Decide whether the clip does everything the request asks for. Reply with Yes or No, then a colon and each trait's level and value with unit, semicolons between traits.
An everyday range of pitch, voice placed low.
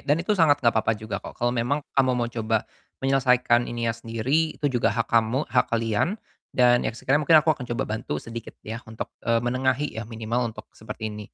Yes: average, 3.0 semitones; low, 120 Hz